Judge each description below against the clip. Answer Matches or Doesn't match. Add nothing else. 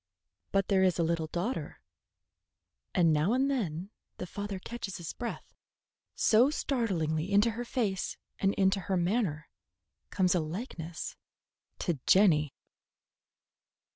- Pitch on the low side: Doesn't match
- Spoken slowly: Matches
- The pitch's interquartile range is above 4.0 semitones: Matches